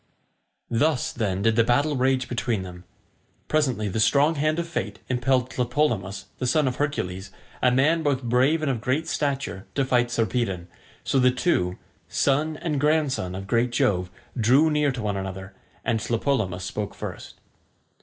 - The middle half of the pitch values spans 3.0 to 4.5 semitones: No, wide, 5.4 semitones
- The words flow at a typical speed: Yes, average, 165 wpm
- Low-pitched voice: Yes, low, 125 Hz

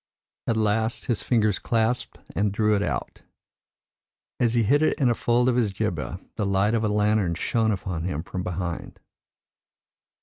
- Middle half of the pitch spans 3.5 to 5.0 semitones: No, average, 3.1 semitones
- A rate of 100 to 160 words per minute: No, average, 170 wpm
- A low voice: Yes, low, 105 Hz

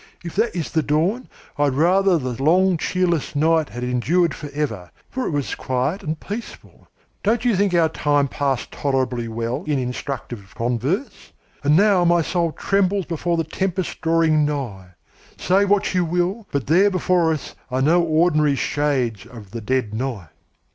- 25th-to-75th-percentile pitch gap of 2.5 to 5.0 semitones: No, wide, 5.4 semitones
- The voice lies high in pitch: No, medium, 155 Hz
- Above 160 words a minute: Yes, average, 170 wpm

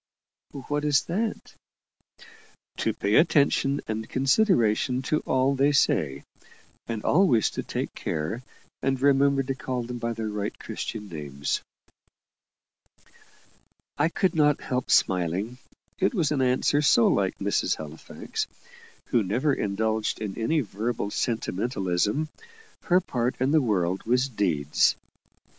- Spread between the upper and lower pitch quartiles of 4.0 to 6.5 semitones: Yes, average, 5.3 semitones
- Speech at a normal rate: No, slow, 125 wpm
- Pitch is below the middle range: Yes, low, 125 Hz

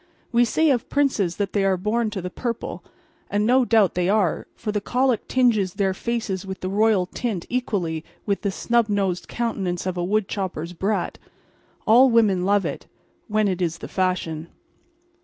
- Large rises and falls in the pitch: No, average, 3.9 semitones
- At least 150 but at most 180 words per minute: Yes, average, 175 wpm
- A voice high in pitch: Yes, high, 205 Hz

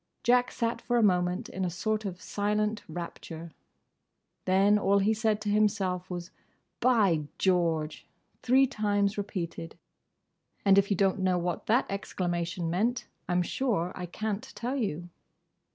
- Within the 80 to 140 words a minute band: No, average, 150 wpm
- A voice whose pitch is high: Yes, high, 195 Hz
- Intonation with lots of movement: No, average, 3.4 semitones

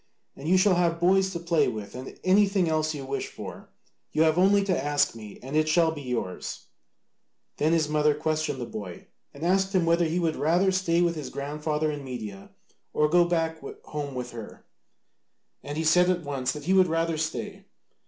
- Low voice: No, medium, 160 Hz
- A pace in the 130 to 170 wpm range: No, average, 200 wpm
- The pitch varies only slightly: No, average, 3.6 semitones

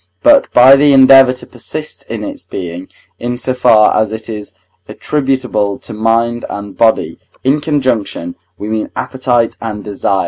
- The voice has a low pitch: Yes, low, 120 Hz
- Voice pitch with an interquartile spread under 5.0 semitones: Yes, average, 3.8 semitones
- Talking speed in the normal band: Yes, average, 165 wpm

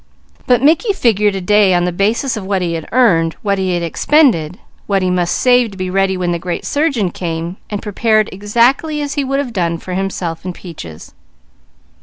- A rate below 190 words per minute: No, fast, 205 wpm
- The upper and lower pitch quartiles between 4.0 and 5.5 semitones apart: Yes, average, 5.1 semitones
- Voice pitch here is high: Yes, high, 195 Hz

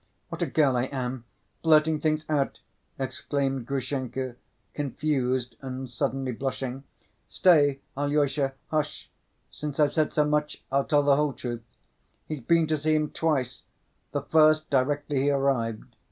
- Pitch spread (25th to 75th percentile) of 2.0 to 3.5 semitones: Yes, narrow, 2.5 semitones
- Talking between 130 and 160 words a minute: Yes, average, 140 wpm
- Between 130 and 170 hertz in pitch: Yes, medium, 140 Hz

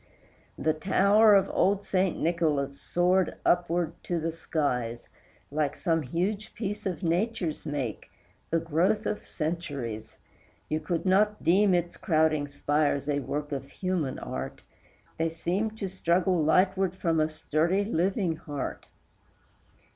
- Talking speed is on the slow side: Yes, slow, 130 wpm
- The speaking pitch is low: No, medium, 170 Hz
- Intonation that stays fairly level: No, average, 3.8 semitones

